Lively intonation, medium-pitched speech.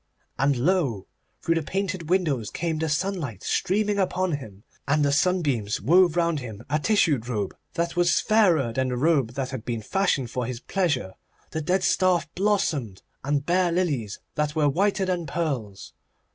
Yes: wide, 6.2 semitones; medium, 155 Hz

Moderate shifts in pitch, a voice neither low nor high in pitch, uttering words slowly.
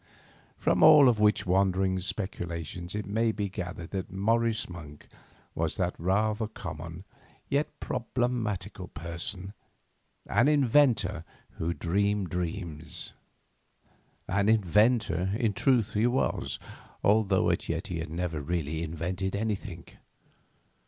No: average, 4.0 semitones; very low, 95 Hz; slow, 115 wpm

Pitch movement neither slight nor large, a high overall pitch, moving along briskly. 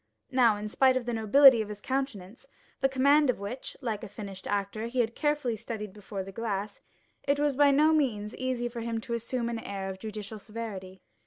Yes: average, 3.9 semitones; high, 230 Hz; fast, 210 wpm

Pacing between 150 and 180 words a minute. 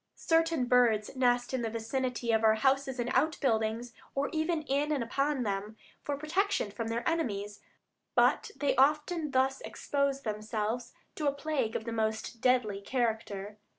Yes: average, 155 wpm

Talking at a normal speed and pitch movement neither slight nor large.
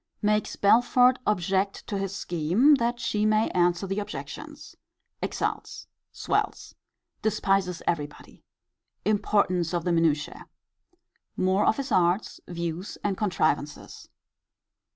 No: slow, 110 wpm; average, 3.5 semitones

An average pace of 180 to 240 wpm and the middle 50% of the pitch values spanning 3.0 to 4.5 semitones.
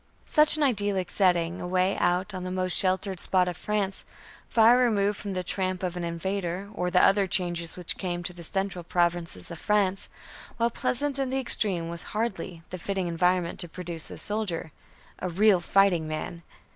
No: average, 185 wpm; narrow, 2.5 semitones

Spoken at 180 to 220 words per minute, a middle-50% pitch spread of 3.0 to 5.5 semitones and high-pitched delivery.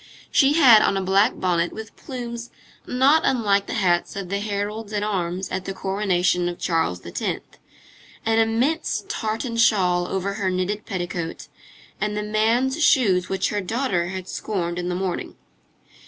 No: average, 160 wpm; average, 3.6 semitones; high, 200 Hz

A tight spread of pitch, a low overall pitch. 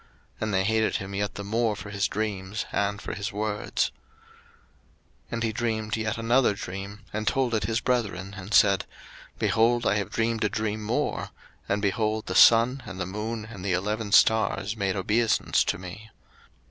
Yes: narrow, 2.1 semitones; low, 105 Hz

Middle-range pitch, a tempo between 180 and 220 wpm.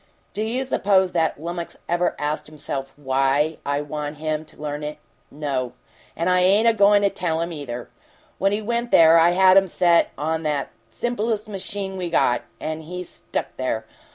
Yes: medium, 165 Hz; average, 185 wpm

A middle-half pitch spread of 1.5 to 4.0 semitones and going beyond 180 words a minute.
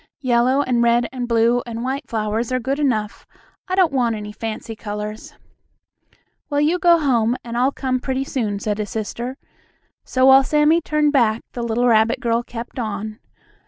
No: average, 3.2 semitones; average, 175 wpm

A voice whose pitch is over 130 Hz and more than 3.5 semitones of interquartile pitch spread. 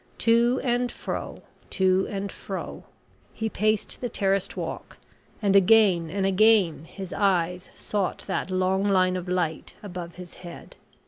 No: high, 190 Hz; average, 2.7 semitones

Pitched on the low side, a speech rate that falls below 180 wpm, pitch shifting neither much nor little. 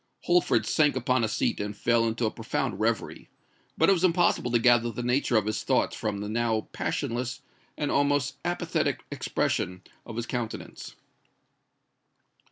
Yes: low, 120 Hz; average, 160 wpm; average, 4.2 semitones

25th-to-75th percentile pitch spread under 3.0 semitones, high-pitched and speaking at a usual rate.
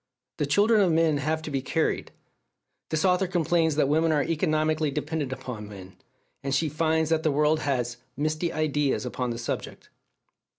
No: narrow, 2.6 semitones; medium, 155 Hz; average, 170 wpm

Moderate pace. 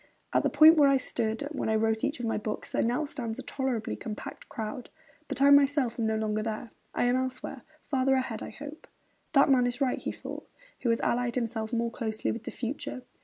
No: fast, 220 wpm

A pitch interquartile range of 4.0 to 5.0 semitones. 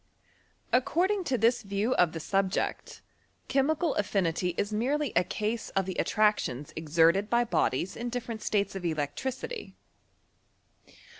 No: wide, 5.6 semitones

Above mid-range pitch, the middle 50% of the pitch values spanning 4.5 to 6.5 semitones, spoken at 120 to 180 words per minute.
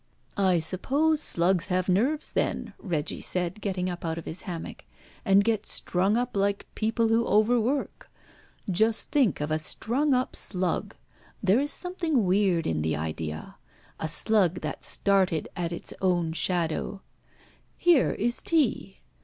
Yes: high, 195 Hz; average, 5.1 semitones; average, 150 wpm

